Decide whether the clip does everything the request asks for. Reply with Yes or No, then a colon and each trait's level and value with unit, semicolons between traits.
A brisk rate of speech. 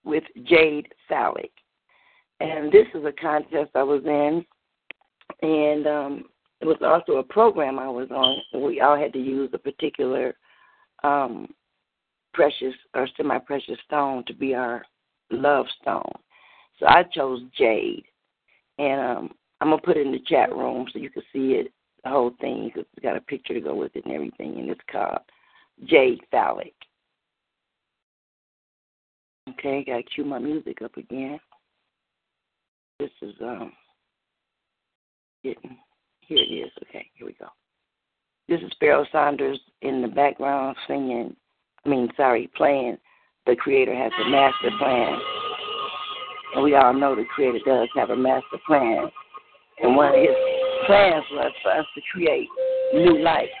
No: average, 150 wpm